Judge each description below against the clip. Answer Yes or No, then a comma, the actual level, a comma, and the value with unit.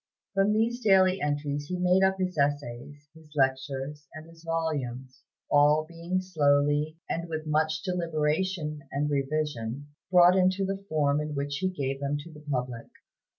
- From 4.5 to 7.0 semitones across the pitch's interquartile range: No, average, 3.9 semitones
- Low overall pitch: No, medium, 150 Hz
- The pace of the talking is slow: No, average, 155 wpm